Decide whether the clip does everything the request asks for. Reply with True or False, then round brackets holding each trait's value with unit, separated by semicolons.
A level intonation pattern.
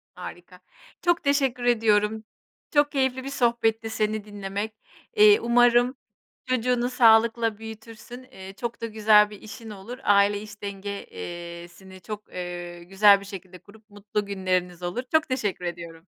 False (3.6 semitones)